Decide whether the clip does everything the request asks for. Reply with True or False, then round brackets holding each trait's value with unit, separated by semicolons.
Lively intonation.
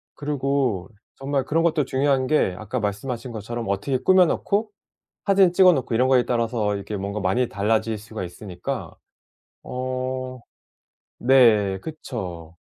False (4.9 semitones)